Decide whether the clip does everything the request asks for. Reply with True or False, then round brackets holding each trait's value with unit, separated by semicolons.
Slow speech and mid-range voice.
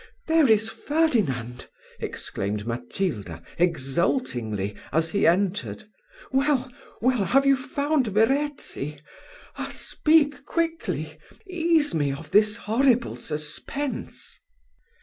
False (95 wpm; 220 Hz)